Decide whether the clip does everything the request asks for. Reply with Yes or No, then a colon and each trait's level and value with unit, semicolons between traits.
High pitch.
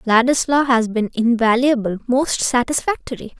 Yes: high, 245 Hz